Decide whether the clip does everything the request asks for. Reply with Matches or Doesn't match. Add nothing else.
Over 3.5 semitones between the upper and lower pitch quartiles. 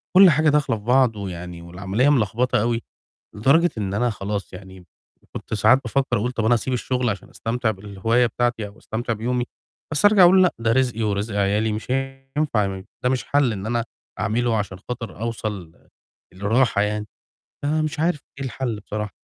Matches